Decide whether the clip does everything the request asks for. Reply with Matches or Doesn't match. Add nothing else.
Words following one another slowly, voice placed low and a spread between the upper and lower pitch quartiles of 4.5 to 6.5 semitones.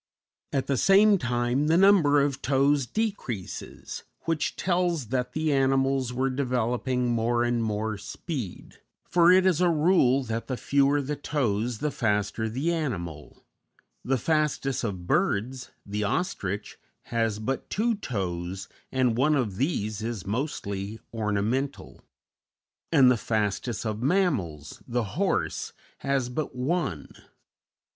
Matches